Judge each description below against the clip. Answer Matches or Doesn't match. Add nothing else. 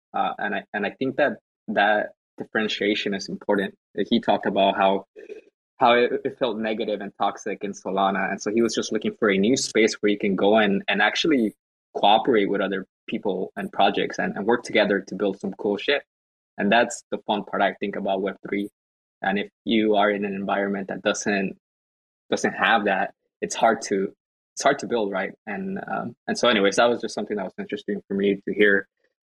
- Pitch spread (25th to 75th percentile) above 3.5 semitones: Doesn't match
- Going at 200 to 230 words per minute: Matches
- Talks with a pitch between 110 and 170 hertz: Doesn't match